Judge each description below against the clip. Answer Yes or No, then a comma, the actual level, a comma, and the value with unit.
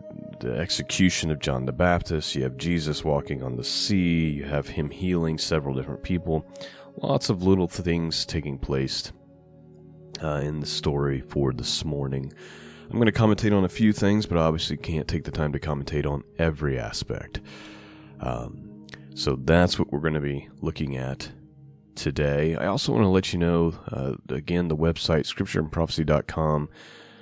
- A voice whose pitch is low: Yes, very low, 80 Hz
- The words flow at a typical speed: Yes, average, 170 wpm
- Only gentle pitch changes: No, average, 3.4 semitones